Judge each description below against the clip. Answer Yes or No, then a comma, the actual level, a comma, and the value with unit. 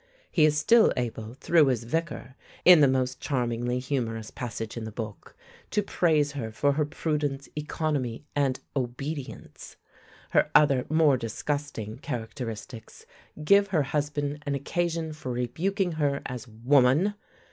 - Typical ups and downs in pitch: Yes, average, 3.8 semitones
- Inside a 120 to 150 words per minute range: Yes, slow, 135 wpm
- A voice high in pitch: No, medium, 140 Hz